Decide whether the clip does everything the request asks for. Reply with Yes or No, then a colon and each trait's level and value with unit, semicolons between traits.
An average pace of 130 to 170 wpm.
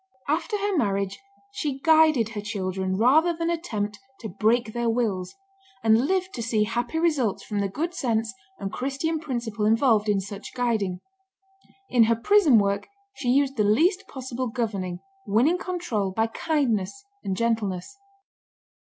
Yes: average, 150 wpm